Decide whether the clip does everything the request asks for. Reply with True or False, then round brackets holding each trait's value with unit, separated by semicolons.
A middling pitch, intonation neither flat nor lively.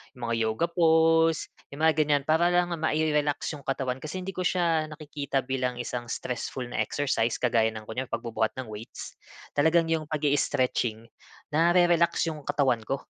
True (145 Hz; 4.4 semitones)